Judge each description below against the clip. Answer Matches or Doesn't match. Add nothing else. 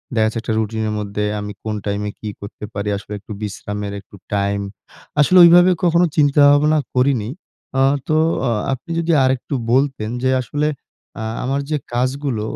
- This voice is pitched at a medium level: Doesn't match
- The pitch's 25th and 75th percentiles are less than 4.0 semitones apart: Doesn't match